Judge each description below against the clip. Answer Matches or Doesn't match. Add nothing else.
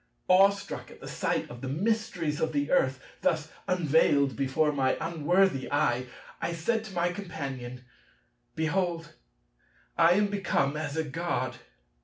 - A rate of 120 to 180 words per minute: Matches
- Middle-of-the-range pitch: Matches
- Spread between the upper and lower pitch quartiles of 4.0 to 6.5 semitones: Matches